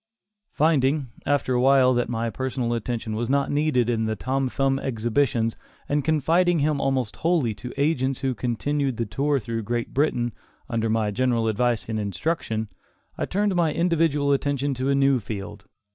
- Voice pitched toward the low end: Yes, low, 130 Hz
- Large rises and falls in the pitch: No, average, 3.8 semitones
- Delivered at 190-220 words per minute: No, average, 170 wpm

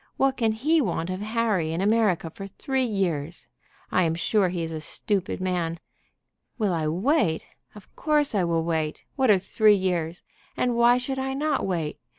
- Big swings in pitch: Yes, wide, 6.0 semitones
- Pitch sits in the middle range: No, high, 195 Hz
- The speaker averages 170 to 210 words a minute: Yes, average, 180 wpm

